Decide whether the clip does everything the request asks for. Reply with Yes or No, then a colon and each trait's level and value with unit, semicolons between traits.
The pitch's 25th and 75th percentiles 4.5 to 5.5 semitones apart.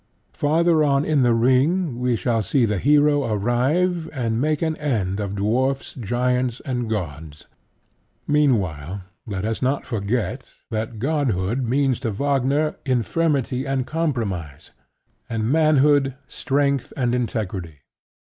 Yes: average, 4.8 semitones